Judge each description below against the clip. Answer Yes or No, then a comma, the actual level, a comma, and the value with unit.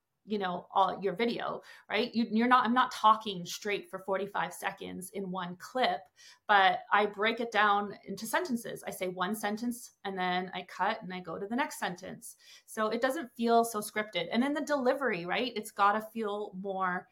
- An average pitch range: Yes, average, 3.8 semitones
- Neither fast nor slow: Yes, average, 195 wpm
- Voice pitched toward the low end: No, high, 210 Hz